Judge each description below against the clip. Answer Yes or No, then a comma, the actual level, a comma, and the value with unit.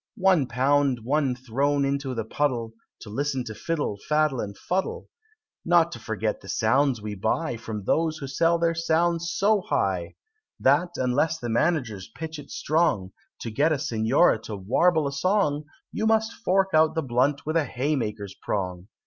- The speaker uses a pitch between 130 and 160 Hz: Yes, medium, 140 Hz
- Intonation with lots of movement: Yes, wide, 6.0 semitones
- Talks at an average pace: Yes, average, 170 wpm